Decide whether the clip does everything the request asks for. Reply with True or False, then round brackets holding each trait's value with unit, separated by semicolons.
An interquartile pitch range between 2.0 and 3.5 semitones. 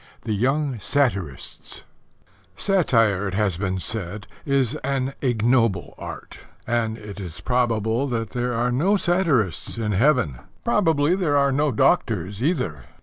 False (5.2 semitones)